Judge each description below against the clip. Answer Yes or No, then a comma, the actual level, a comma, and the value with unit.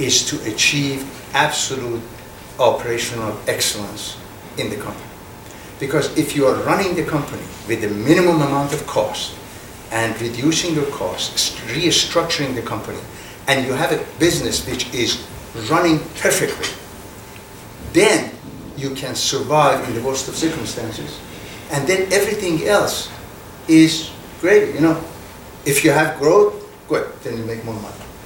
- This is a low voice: Yes, low, 125 Hz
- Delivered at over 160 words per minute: No, average, 140 wpm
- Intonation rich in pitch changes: Yes, wide, 6.4 semitones